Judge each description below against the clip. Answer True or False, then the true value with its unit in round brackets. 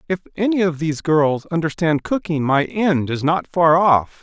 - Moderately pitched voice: True (165 Hz)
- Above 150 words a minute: True (185 wpm)